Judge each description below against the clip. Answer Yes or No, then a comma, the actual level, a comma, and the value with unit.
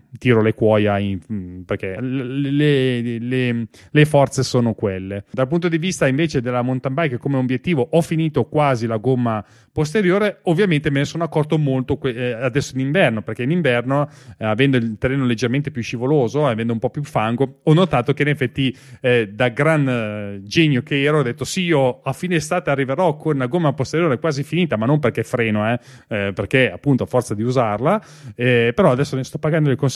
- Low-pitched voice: Yes, low, 130 Hz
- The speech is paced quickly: Yes, fast, 195 wpm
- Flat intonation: No, average, 4.0 semitones